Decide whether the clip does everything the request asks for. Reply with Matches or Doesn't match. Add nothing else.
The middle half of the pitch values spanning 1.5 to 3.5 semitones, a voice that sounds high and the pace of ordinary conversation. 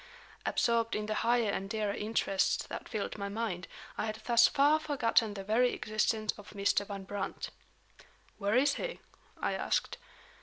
Matches